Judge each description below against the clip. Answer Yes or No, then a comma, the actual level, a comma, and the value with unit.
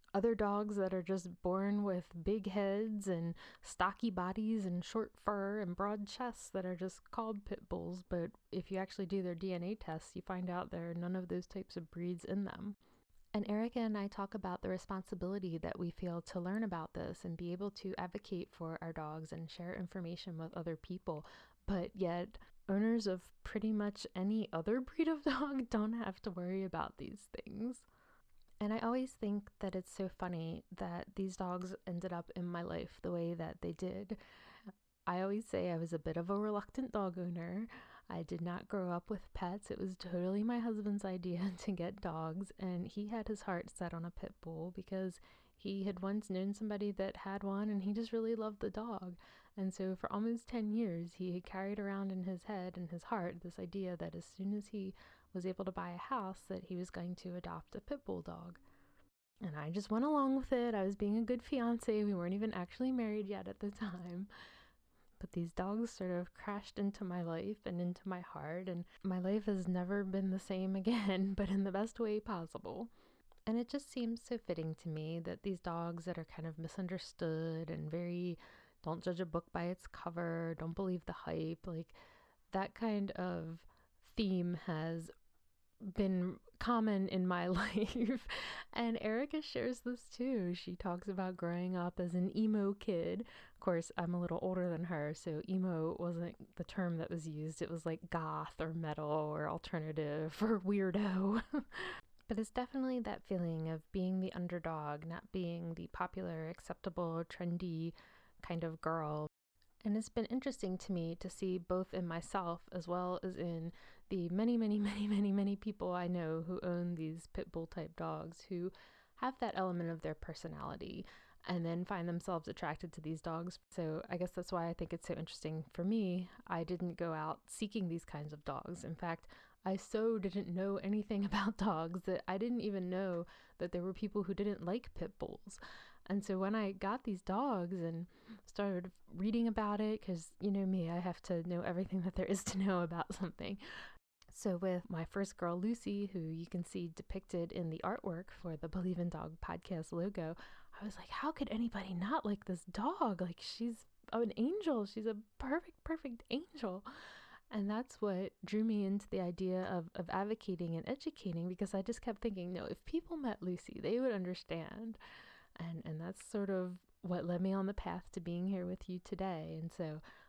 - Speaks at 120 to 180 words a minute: No, average, 195 wpm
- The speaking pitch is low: No, medium, 185 Hz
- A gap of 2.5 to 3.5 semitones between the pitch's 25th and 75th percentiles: Yes, average, 3.1 semitones